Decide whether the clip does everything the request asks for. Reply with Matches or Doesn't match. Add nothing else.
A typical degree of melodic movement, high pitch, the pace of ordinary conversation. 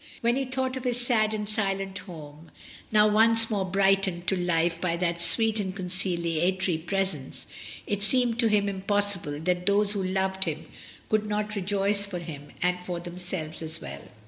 Matches